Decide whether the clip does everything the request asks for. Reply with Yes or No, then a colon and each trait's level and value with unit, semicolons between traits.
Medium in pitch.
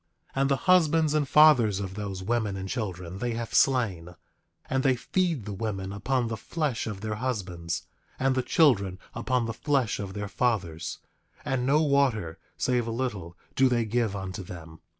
No: low, 115 Hz